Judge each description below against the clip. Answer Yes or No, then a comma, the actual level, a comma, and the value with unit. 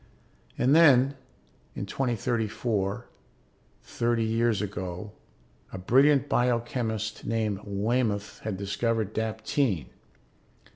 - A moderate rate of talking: No, slow, 85 wpm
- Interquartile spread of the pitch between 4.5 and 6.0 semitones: No, average, 3.0 semitones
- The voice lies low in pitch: Yes, low, 110 Hz